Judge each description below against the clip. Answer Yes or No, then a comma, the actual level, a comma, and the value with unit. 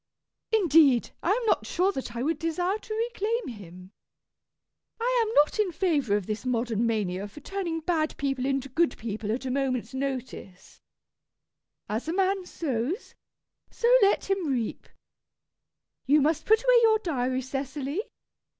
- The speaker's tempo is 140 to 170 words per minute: Yes, average, 150 wpm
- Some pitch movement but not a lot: No, wide, 7.8 semitones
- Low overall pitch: No, very high, 285 Hz